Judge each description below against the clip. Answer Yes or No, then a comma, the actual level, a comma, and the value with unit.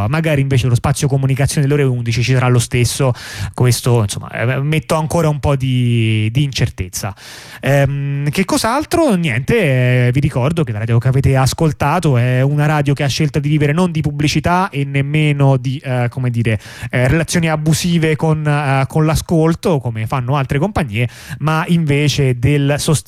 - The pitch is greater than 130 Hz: Yes, medium, 140 Hz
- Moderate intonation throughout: Yes, average, 3.6 semitones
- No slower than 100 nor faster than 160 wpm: No, fast, 170 wpm